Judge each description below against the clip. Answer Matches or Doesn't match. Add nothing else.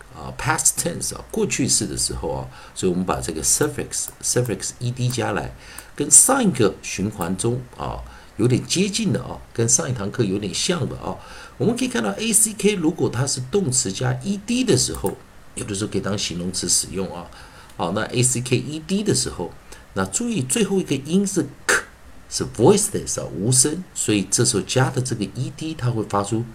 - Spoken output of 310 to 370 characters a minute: Matches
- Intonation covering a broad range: Matches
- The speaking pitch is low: Matches